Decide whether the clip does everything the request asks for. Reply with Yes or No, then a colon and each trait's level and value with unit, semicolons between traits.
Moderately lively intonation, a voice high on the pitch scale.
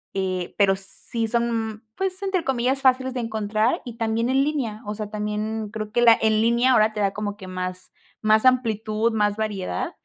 No: narrow, 2.3 semitones; high, 220 Hz